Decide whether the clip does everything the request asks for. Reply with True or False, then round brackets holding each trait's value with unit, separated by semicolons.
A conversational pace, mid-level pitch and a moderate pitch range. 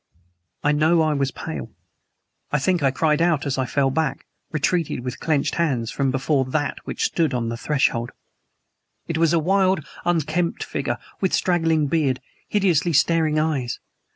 True (165 wpm; 150 Hz; 3.6 semitones)